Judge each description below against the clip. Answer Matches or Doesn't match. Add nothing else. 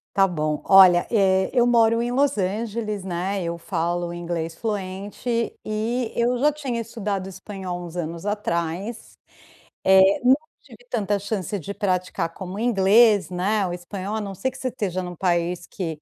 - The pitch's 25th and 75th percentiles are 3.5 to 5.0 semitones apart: Matches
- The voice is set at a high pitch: Matches